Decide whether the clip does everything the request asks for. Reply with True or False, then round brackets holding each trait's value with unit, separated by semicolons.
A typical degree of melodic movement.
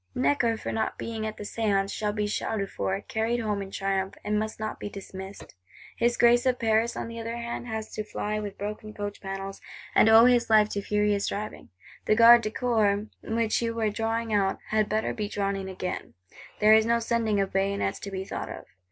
False (2.2 semitones)